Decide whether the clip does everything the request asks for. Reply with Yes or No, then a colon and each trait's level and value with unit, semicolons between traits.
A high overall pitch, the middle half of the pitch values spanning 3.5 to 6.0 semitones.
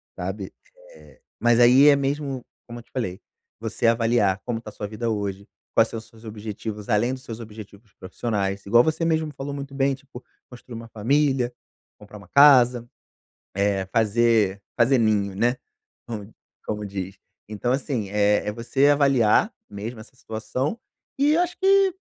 No: low, 115 Hz; average, 4.2 semitones